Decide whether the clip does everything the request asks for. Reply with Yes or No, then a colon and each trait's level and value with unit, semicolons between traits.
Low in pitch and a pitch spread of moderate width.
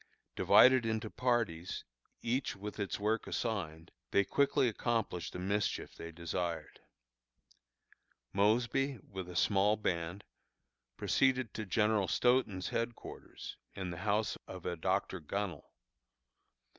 Yes: low, 100 Hz; average, 4.3 semitones